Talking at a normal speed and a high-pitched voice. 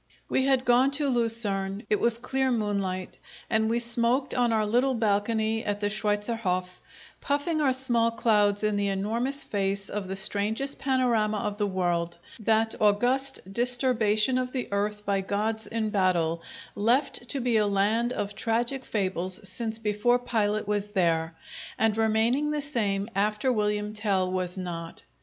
Yes: average, 155 wpm; high, 215 Hz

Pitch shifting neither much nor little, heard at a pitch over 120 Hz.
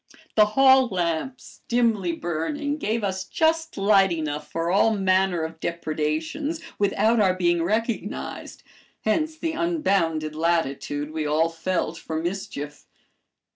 No: wide, 6.0 semitones; medium, 185 Hz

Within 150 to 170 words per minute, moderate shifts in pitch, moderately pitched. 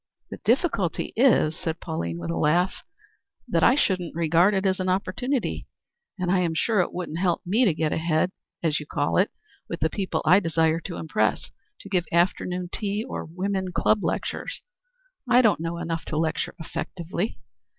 No: average, 180 wpm; average, 3.3 semitones; medium, 175 Hz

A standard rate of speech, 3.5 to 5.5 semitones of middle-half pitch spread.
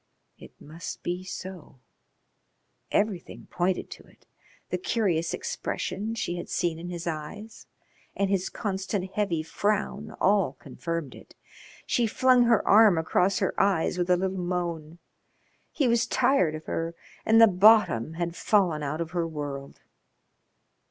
Yes: average, 145 wpm; average, 3.9 semitones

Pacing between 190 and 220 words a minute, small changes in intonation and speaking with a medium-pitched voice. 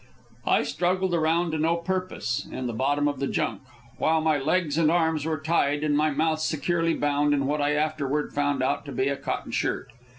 Yes: fast, 205 wpm; narrow, 2.2 semitones; medium, 150 Hz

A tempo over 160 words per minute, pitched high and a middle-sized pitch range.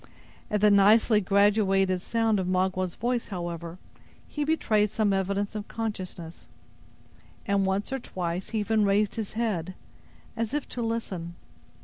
No: average, 140 wpm; high, 200 Hz; average, 3.0 semitones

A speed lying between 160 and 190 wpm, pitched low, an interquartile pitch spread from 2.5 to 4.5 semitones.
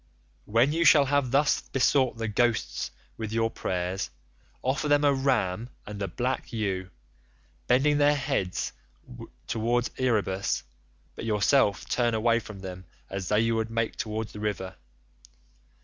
No: average, 145 wpm; low, 115 Hz; average, 4.2 semitones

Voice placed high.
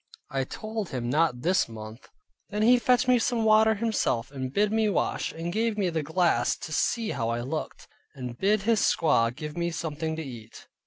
No: medium, 165 Hz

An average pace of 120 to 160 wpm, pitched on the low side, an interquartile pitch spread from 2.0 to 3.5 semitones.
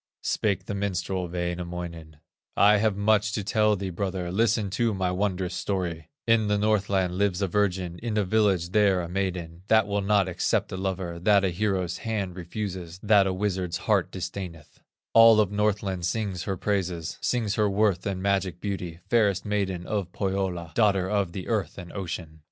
No: average, 175 wpm; very low, 95 Hz; narrow, 2.6 semitones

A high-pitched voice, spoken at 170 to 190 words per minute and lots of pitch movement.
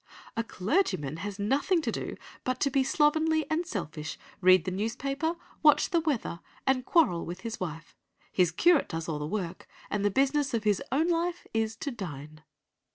Yes: high, 230 Hz; average, 180 wpm; wide, 8.6 semitones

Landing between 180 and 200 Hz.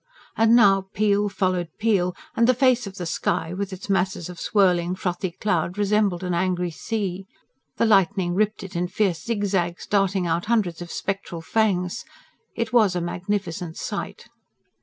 Yes: high, 190 Hz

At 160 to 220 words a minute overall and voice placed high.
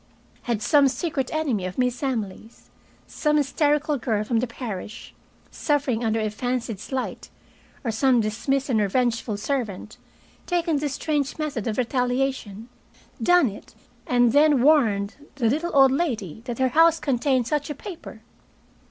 No: average, 145 wpm; very high, 255 Hz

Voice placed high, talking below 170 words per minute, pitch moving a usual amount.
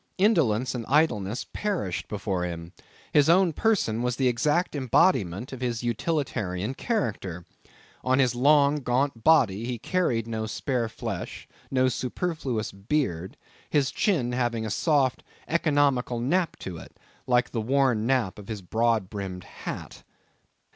No: low, 125 Hz; average, 140 wpm; average, 4.9 semitones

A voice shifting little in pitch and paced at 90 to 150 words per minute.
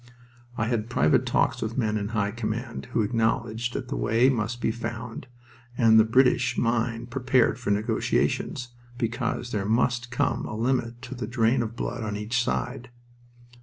No: narrow, 1.8 semitones; average, 165 wpm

